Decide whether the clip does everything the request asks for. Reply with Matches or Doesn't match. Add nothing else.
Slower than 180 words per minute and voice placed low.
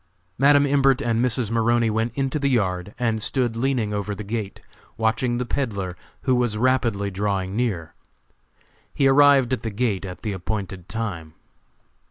Matches